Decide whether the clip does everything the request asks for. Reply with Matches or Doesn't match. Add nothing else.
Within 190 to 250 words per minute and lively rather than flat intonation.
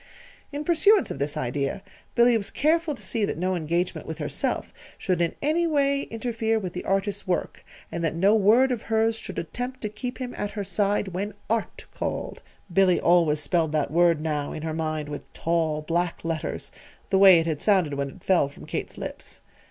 Matches